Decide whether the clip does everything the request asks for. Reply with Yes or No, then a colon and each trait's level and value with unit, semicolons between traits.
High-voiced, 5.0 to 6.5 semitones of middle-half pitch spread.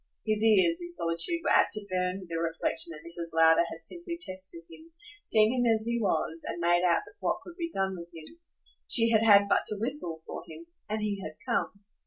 Yes: high, 195 Hz; wide, 5.4 semitones